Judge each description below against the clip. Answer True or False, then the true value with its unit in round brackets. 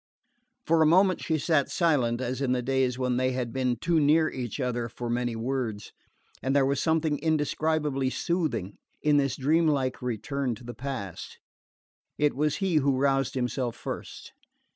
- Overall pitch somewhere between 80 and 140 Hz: True (135 Hz)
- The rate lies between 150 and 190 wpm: True (165 wpm)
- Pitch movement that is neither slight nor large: True (3.5 semitones)